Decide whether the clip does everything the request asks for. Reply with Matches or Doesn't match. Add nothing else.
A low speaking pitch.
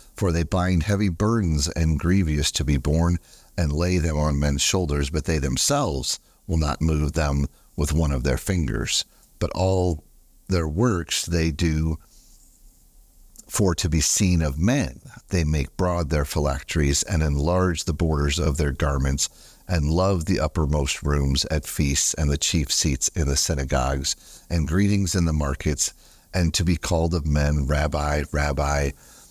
Matches